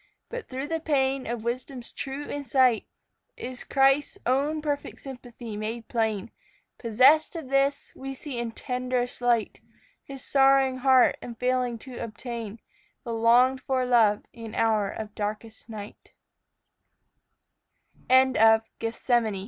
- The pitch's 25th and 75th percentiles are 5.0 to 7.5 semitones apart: No, average, 2.9 semitones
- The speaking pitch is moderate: No, very high, 250 Hz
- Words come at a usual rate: No, slow, 130 wpm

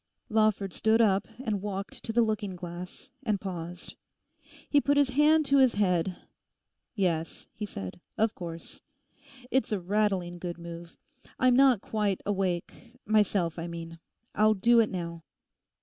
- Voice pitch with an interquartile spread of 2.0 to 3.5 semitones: No, average, 4.2 semitones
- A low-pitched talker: No, high, 200 Hz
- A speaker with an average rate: Yes, average, 150 wpm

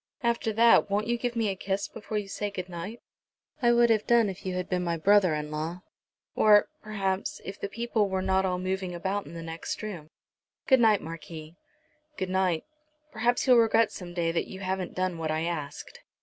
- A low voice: No, high, 190 Hz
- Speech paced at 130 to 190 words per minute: No, fast, 205 wpm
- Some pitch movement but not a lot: Yes, average, 3.7 semitones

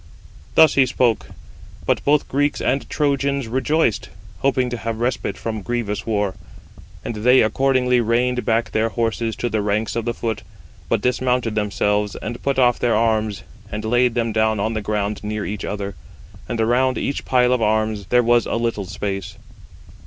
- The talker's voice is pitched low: Yes, low, 115 Hz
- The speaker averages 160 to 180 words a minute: Yes, average, 175 wpm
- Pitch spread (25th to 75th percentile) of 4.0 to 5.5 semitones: No, average, 2.7 semitones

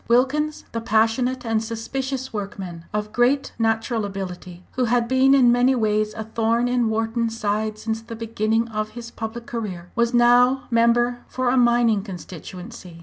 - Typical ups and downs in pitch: No, narrow, 2.2 semitones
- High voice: Yes, high, 230 Hz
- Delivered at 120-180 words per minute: Yes, average, 160 wpm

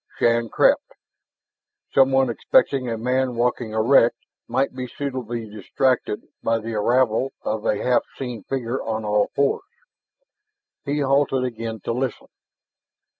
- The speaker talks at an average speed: No, slow, 125 wpm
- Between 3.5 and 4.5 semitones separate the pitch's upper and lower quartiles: No, average, 2.7 semitones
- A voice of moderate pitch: No, low, 125 Hz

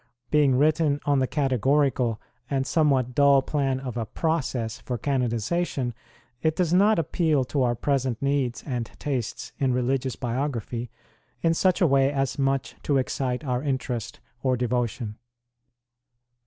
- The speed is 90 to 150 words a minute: Yes, average, 140 wpm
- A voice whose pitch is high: No, low, 135 Hz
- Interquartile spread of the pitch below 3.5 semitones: Yes, average, 2.8 semitones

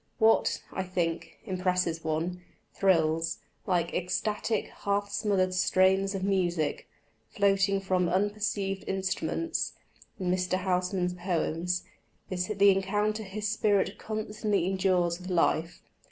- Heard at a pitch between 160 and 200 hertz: Yes, high, 190 Hz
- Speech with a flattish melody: Yes, narrow, 2.1 semitones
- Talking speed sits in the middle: No, slow, 110 wpm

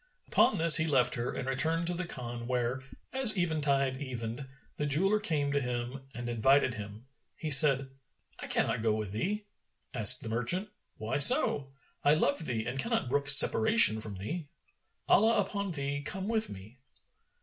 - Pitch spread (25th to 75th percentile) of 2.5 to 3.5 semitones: No, wide, 5.6 semitones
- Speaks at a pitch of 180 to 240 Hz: No, low, 135 Hz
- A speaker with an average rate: Yes, average, 170 wpm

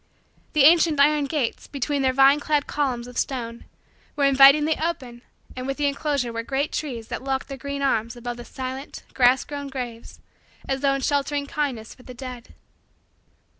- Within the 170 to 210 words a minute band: Yes, average, 175 wpm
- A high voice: Yes, very high, 270 Hz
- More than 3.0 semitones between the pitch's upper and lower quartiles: No, narrow, 2.5 semitones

